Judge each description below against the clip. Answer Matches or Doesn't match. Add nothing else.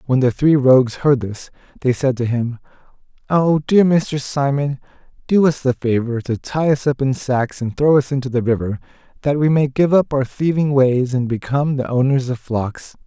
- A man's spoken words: Matches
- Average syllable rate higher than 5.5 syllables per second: Doesn't match